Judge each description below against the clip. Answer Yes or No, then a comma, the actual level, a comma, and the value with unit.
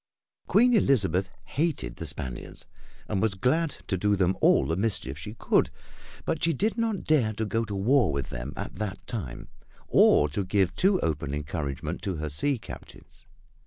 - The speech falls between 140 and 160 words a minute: No, average, 175 wpm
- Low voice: Yes, low, 100 Hz